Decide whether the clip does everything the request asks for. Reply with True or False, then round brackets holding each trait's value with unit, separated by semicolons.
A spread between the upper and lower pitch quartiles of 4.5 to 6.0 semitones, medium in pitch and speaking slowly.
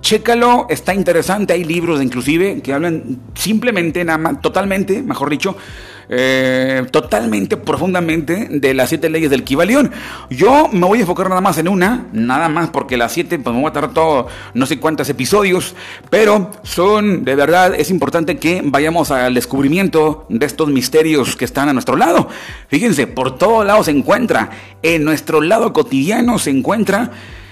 False (5.3 semitones; 165 Hz; 170 wpm)